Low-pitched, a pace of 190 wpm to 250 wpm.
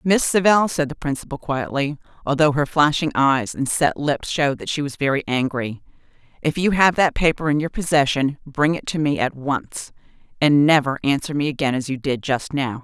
No: medium, 145 Hz; average, 200 wpm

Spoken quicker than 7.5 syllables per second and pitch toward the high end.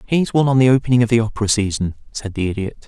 No: 7.8 syllables/s; low, 115 Hz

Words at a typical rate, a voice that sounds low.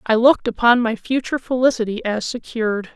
No: average, 160 wpm; high, 235 Hz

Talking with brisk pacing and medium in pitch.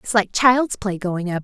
No: fast, 250 wpm; high, 205 Hz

